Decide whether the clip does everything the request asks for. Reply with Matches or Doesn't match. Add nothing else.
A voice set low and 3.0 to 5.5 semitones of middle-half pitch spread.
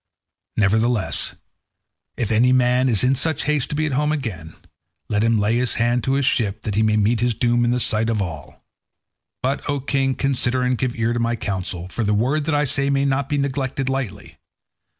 Matches